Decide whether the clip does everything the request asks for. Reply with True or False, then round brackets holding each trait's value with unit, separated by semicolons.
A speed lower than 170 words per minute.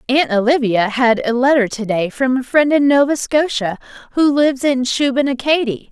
True (160 wpm)